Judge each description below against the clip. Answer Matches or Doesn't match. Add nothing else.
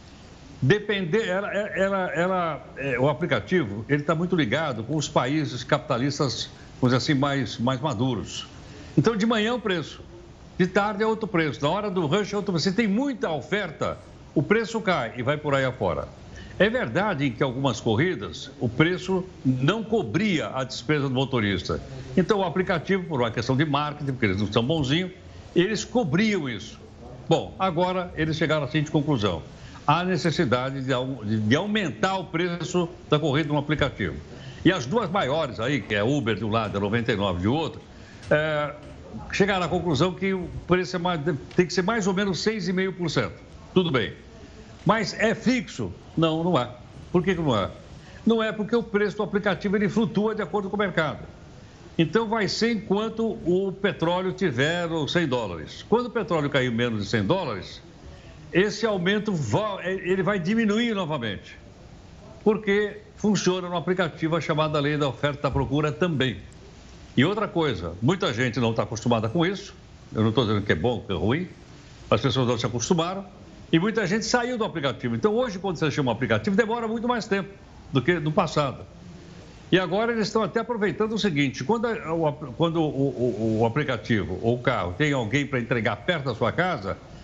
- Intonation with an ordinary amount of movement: Doesn't match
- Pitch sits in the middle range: Matches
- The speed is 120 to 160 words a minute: Doesn't match